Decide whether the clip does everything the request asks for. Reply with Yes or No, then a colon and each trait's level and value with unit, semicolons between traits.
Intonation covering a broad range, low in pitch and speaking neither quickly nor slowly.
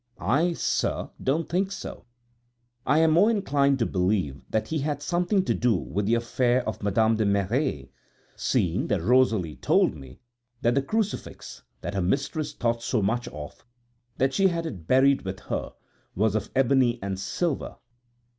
Yes: wide, 6.6 semitones; low, 120 Hz; average, 165 wpm